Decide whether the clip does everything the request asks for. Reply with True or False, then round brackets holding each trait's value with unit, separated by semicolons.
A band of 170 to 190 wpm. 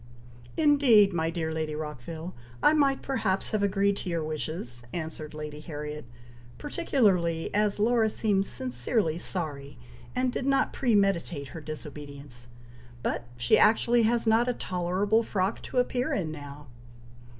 False (140 wpm)